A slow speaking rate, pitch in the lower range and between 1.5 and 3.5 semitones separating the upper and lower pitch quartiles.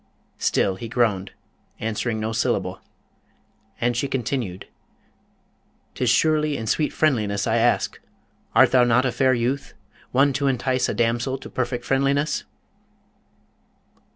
Yes: slow, 125 wpm; low, 125 Hz; average, 2.9 semitones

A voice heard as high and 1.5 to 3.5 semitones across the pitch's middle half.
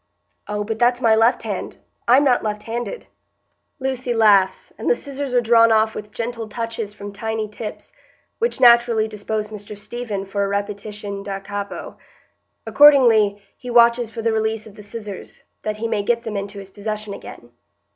Yes: high, 220 Hz; narrow, 2.4 semitones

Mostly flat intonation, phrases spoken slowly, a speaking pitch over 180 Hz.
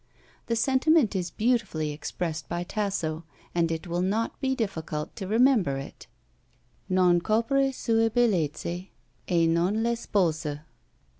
No: wide, 5.6 semitones; slow, 125 wpm; high, 190 Hz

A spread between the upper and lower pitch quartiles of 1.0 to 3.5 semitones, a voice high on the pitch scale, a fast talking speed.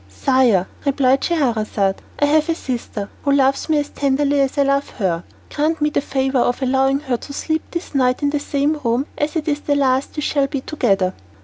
Yes: narrow, 2.4 semitones; very high, 275 Hz; fast, 210 wpm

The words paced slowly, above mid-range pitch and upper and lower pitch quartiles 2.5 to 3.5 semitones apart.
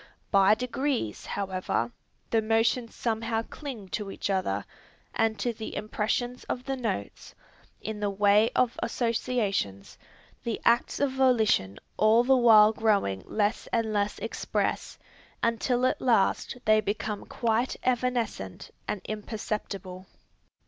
Yes: slow, 125 wpm; high, 220 Hz; average, 2.9 semitones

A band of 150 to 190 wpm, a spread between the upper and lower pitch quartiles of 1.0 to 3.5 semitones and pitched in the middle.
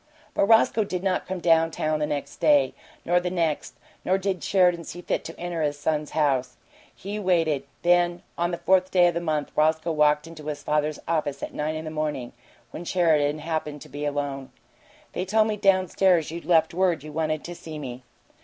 No: fast, 205 wpm; average, 2.9 semitones; medium, 160 Hz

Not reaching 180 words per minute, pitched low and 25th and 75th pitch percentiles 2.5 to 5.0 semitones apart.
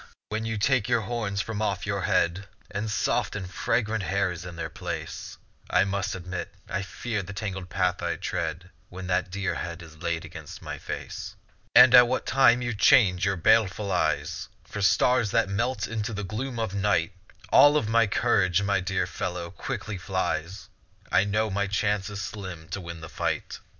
No: average, 185 wpm; low, 100 Hz; average, 3.2 semitones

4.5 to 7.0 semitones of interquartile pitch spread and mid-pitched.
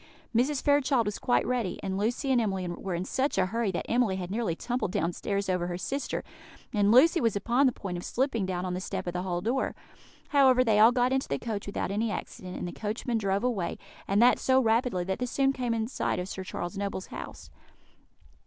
No: average, 5.0 semitones; high, 215 Hz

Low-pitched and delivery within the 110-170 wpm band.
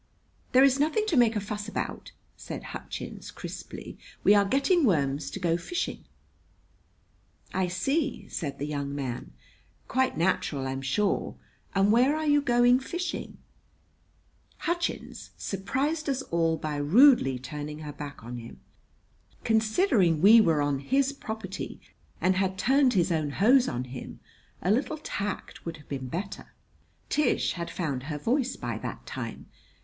No: high, 195 Hz; average, 150 wpm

